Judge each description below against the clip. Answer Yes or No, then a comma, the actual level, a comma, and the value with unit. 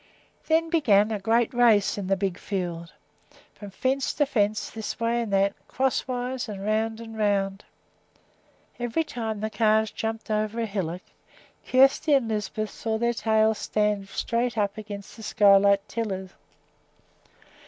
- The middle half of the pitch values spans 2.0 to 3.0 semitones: Yes, average, 2.7 semitones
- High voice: Yes, high, 215 Hz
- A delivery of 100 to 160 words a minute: Yes, average, 150 wpm